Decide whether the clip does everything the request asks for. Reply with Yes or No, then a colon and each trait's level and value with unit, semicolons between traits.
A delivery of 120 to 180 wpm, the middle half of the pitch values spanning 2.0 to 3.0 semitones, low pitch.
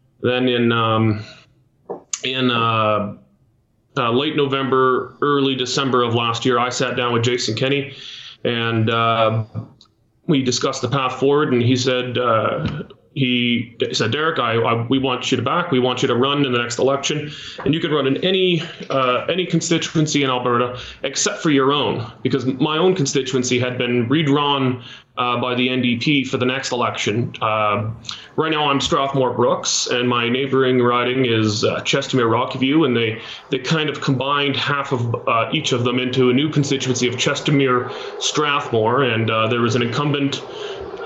Yes: average, 170 wpm; narrow, 2.6 semitones; low, 130 Hz